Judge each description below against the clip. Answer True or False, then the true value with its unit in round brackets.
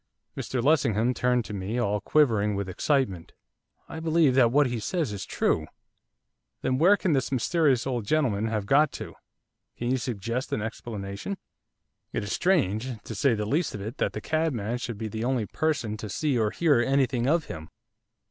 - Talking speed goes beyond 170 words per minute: True (185 wpm)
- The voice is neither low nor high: False (120 Hz)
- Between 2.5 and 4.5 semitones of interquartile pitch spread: False (5.2 semitones)